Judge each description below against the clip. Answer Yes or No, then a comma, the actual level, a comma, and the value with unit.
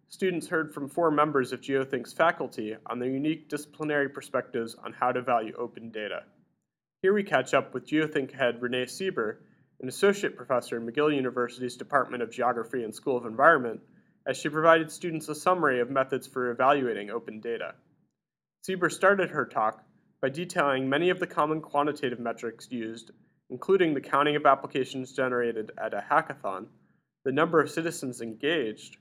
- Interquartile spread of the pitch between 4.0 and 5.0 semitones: Yes, average, 4.3 semitones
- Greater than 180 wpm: No, average, 165 wpm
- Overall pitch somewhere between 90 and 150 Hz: Yes, medium, 140 Hz